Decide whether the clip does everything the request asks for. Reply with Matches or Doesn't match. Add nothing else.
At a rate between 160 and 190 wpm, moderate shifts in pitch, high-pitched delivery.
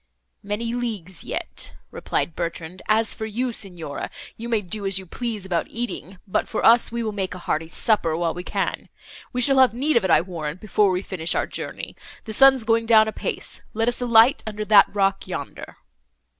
Doesn't match